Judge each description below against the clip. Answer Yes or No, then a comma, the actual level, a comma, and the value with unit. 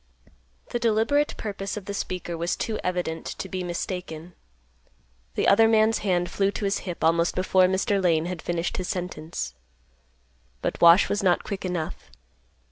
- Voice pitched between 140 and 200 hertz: Yes, medium, 185 Hz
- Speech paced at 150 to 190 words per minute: Yes, average, 160 wpm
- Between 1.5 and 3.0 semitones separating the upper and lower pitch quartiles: Yes, average, 2.7 semitones